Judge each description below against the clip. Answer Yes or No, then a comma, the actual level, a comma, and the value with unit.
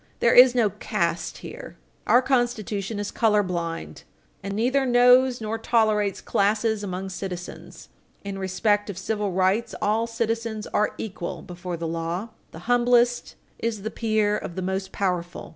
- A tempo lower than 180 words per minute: Yes, average, 150 wpm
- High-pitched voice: Yes, high, 210 Hz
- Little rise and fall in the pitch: No, average, 3.6 semitones